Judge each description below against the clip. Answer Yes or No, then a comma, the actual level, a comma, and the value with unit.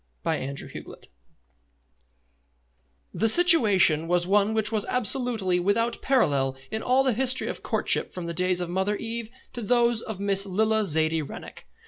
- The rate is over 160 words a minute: No, average, 150 wpm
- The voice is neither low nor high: No, high, 205 Hz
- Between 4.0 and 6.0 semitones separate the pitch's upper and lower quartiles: Yes, average, 4.8 semitones